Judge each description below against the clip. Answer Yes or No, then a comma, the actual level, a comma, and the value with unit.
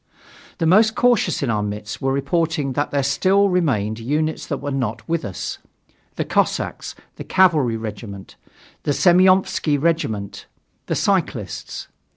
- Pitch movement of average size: No, wide, 7.4 semitones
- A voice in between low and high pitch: Yes, medium, 145 Hz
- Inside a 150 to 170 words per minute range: No, average, 140 wpm